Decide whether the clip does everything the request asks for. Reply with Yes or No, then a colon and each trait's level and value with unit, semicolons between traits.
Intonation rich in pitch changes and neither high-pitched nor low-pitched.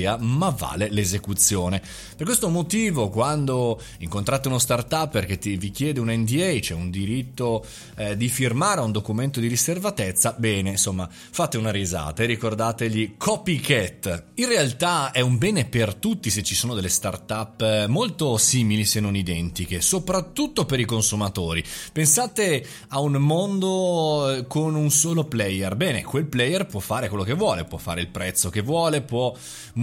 No: wide, 6.8 semitones; low, 115 Hz